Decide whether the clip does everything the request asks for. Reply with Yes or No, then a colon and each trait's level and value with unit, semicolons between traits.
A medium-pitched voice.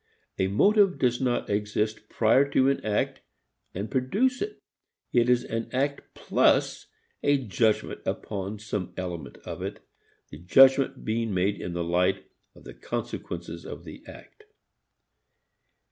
No: low, 110 Hz